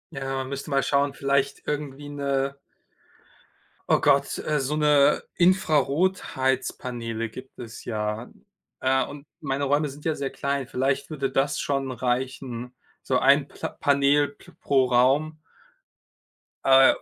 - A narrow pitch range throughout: Yes, narrow, 1.5 semitones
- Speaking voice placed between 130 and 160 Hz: Yes, low, 135 Hz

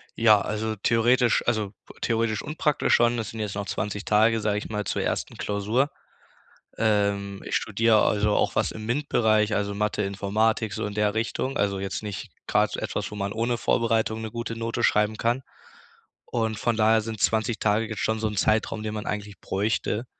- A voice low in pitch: Yes, low, 110 Hz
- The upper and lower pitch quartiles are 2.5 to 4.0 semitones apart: No, narrow, 1.6 semitones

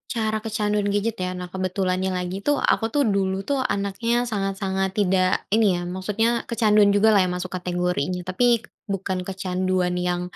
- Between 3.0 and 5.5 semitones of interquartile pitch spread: No, narrow, 2.4 semitones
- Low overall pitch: No, high, 190 Hz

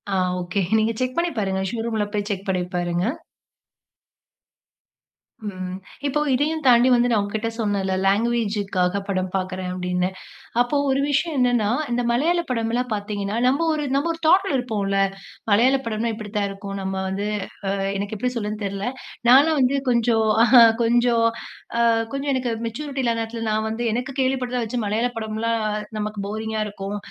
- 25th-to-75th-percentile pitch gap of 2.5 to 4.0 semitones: Yes, average, 3.7 semitones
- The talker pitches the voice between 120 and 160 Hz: No, high, 225 Hz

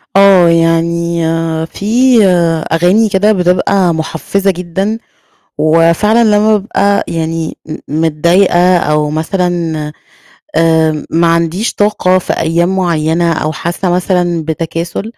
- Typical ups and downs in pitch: Yes, average, 3.1 semitones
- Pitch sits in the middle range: Yes, medium, 175 Hz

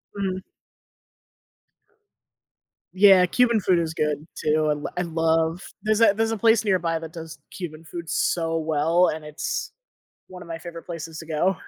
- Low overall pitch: No, medium, 165 Hz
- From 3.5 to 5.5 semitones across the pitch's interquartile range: No, average, 2.7 semitones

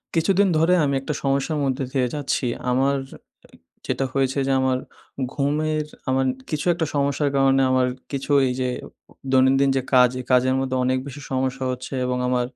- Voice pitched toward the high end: No, low, 135 Hz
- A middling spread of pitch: No, narrow, 1.7 semitones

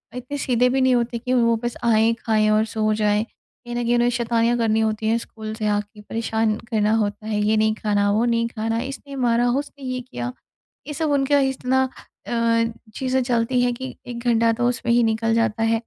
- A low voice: No, high, 230 Hz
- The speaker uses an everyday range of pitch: No, narrow, 2.2 semitones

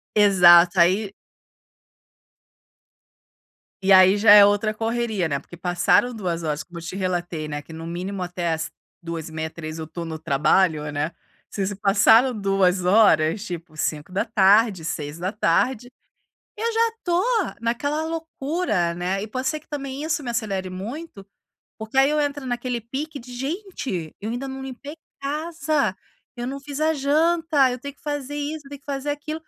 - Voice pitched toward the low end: No, high, 215 Hz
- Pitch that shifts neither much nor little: No, wide, 8.0 semitones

